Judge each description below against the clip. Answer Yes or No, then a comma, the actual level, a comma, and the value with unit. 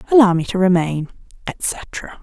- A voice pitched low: No, high, 190 Hz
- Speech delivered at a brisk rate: No, slow, 135 wpm